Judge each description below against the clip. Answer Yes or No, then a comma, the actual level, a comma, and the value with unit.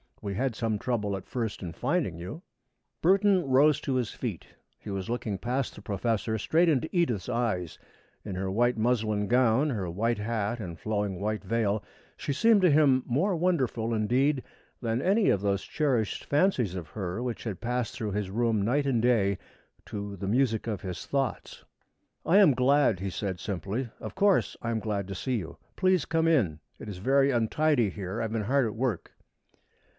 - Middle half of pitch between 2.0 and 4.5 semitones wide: No, average, 5.1 semitones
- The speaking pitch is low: Yes, low, 115 Hz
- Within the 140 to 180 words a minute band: No, average, 190 wpm